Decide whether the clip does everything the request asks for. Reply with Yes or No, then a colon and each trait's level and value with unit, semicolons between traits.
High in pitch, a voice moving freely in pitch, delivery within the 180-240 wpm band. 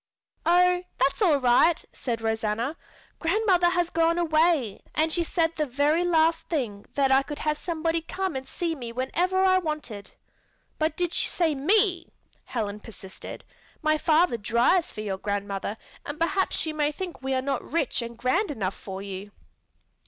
No: very high, 305 Hz; wide, 6.3 semitones; average, 165 wpm